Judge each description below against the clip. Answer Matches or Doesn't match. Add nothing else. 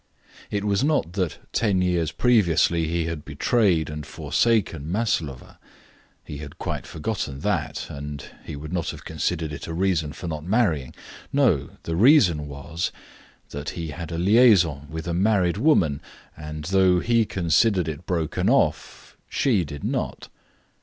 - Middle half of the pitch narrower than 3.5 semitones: Doesn't match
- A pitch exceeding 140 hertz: Doesn't match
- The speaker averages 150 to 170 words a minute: Matches